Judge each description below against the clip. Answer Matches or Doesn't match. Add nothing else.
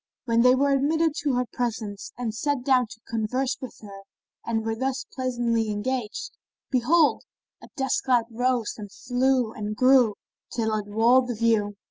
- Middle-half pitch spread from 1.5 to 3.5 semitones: Matches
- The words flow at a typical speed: Matches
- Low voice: Doesn't match